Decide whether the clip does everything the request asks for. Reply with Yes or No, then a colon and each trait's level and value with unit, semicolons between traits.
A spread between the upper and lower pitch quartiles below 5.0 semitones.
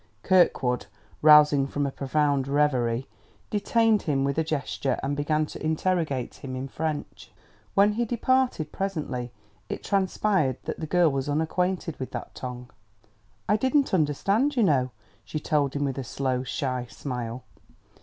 No: wide, 5.5 semitones